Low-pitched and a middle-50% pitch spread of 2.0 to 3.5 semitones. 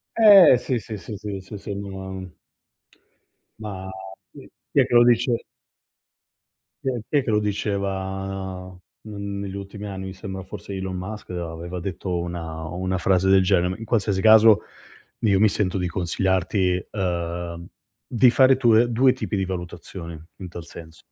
Yes: very low, 95 Hz; average, 2.7 semitones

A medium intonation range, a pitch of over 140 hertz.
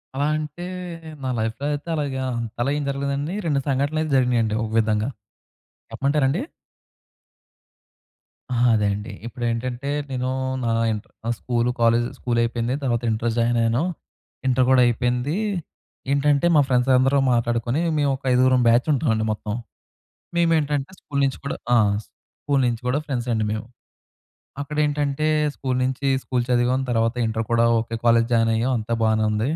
No: average, 3.2 semitones; low, 125 Hz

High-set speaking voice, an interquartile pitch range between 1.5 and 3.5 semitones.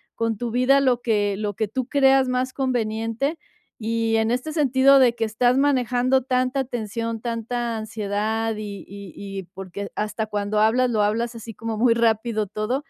Yes: high, 230 Hz; average, 2.9 semitones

